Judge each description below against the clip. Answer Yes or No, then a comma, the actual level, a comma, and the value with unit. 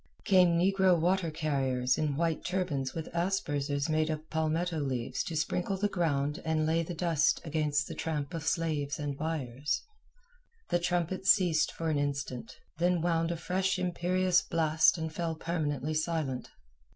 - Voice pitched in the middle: Yes, medium, 160 Hz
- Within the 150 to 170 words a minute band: Yes, average, 155 wpm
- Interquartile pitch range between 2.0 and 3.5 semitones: Yes, average, 3.0 semitones